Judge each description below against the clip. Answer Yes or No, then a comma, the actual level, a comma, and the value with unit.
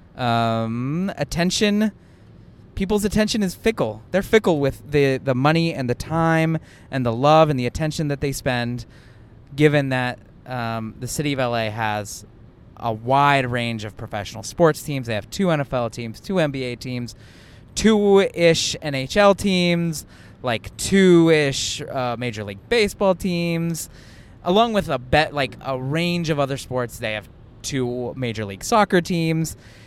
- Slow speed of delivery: No, average, 155 wpm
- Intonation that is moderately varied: No, wide, 6.1 semitones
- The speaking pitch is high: No, low, 135 Hz